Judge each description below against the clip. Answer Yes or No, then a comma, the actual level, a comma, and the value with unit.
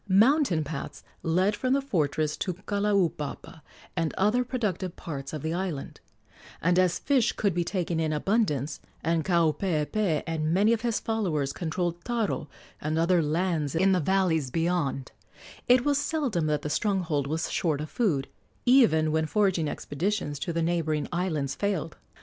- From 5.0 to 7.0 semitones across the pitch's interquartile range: No, average, 4.6 semitones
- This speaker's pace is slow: No, average, 155 wpm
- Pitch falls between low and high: Yes, medium, 170 Hz